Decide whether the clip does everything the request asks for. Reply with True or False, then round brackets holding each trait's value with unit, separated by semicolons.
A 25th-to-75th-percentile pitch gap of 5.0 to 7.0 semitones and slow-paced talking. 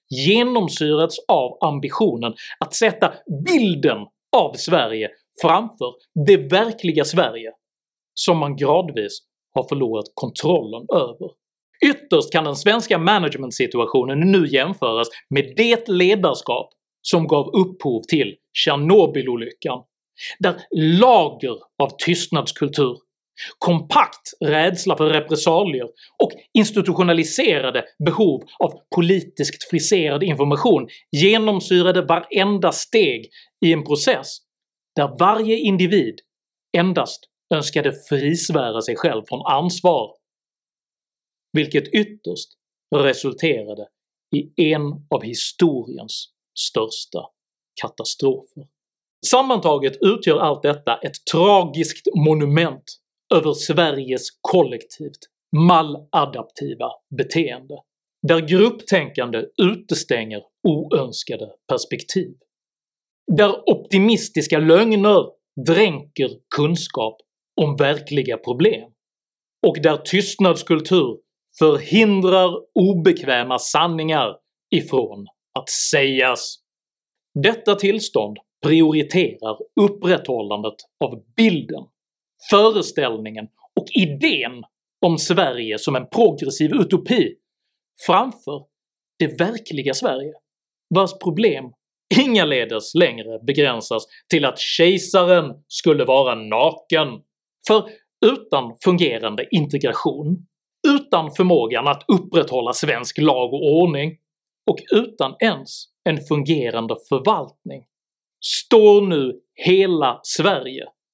True (5.3 semitones; 85 wpm)